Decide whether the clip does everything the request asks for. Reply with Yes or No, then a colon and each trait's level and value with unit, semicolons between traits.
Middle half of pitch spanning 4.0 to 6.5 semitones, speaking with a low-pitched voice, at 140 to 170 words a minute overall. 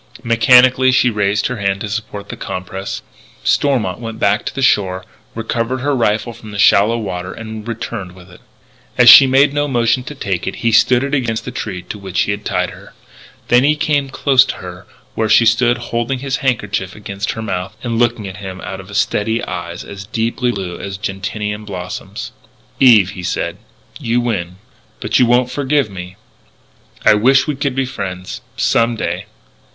No: average, 4.3 semitones; low, 110 Hz; average, 190 wpm